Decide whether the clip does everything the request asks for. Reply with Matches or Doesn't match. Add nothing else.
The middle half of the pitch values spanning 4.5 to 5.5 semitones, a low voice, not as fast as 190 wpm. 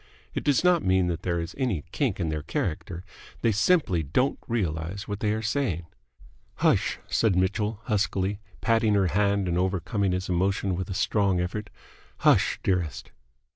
Doesn't match